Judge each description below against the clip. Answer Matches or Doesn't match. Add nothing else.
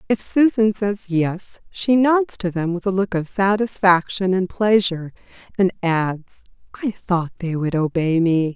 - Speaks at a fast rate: Doesn't match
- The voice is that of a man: Doesn't match